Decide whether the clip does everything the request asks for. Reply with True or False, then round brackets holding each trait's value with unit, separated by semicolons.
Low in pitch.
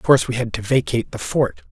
True (125 Hz)